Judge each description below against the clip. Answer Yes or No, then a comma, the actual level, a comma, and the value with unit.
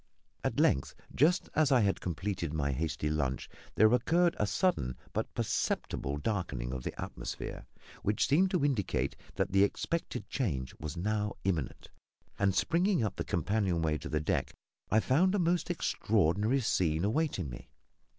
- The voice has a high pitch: No, low, 100 Hz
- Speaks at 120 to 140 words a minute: No, average, 160 wpm